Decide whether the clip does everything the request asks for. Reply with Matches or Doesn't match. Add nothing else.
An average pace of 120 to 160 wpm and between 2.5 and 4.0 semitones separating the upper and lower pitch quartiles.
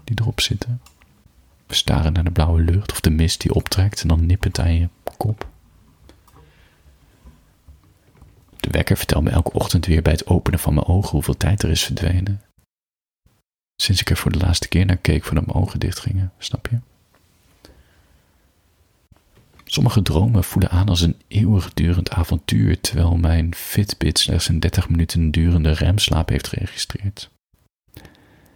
Matches